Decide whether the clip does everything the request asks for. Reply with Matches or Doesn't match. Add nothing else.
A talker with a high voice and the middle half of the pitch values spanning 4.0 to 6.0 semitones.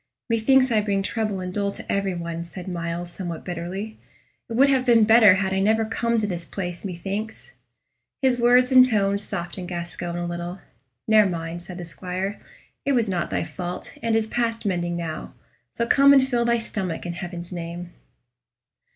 Matches